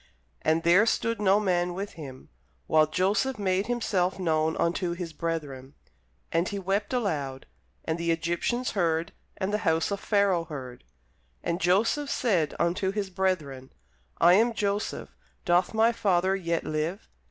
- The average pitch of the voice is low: No, medium, 180 Hz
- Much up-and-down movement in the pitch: No, average, 3.7 semitones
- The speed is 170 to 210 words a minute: No, average, 150 wpm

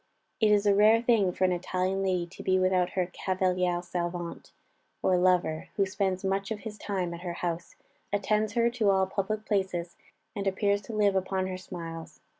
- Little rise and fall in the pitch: Yes, narrow, 2.1 semitones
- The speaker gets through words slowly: No, average, 190 wpm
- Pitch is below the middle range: No, high, 190 Hz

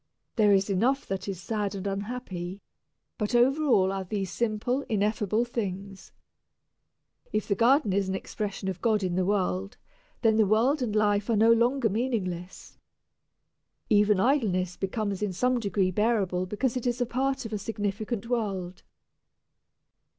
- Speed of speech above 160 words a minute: No, average, 155 wpm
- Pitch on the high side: Yes, high, 210 Hz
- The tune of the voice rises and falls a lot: No, average, 3.5 semitones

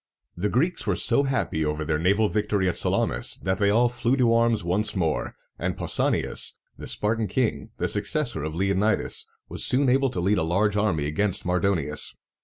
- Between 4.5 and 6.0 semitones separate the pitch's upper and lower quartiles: Yes, average, 5.0 semitones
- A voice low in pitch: Yes, low, 100 Hz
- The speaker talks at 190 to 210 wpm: Yes, average, 195 wpm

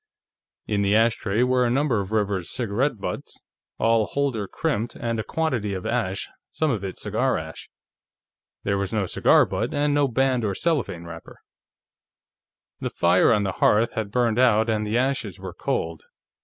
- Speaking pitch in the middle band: No, low, 110 Hz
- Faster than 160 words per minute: Yes, average, 170 wpm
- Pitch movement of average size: Yes, average, 4.1 semitones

